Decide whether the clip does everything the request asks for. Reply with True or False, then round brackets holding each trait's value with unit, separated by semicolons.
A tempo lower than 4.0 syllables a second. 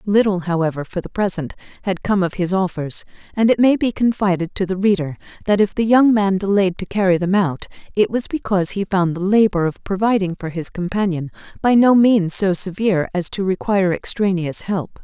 False (5.5 syllables/s)